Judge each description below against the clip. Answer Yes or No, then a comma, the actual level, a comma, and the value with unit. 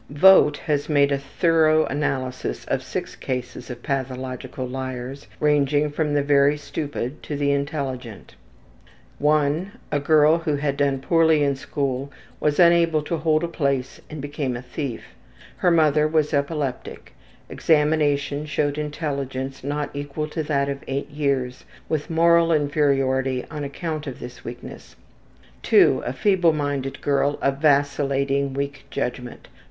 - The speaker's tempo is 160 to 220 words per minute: No, average, 140 wpm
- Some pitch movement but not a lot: No, narrow, 2.0 semitones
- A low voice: No, medium, 145 Hz